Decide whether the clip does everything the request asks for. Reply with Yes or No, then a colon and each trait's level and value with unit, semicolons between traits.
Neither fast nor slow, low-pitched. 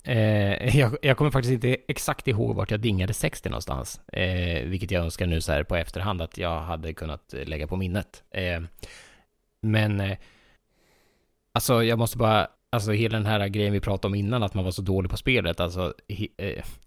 Yes: average, 190 wpm; low, 100 Hz